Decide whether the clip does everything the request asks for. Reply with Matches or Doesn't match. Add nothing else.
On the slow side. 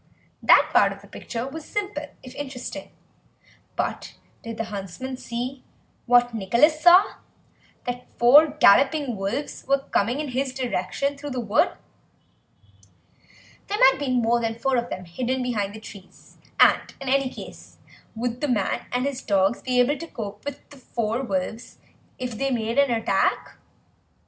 Doesn't match